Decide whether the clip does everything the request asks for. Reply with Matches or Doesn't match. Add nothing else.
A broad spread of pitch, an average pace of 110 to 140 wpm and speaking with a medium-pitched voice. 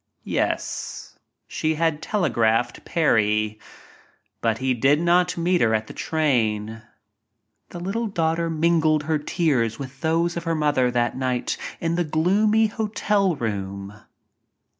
Matches